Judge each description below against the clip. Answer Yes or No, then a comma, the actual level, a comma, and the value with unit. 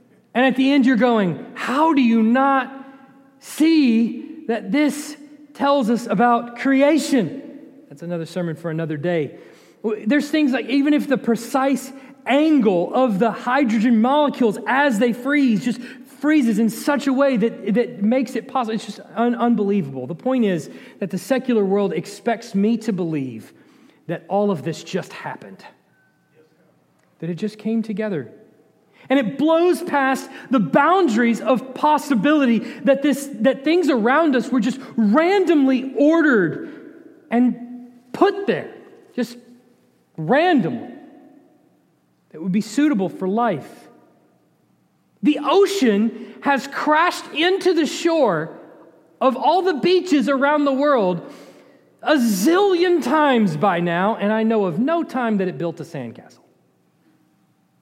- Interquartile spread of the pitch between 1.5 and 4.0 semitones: No, average, 5.1 semitones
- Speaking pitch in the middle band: No, very high, 255 Hz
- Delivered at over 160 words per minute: No, average, 140 wpm